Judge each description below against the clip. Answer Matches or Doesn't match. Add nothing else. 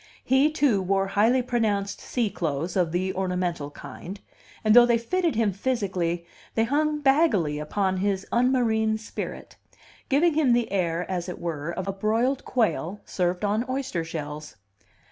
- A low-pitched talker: Doesn't match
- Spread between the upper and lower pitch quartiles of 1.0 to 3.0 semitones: Doesn't match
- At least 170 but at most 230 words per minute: Doesn't match